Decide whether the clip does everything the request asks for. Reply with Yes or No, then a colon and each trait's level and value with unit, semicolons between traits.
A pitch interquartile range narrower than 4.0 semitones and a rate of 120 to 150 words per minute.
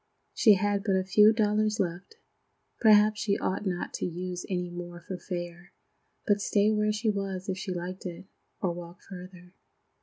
No: average, 2.8 semitones; average, 175 wpm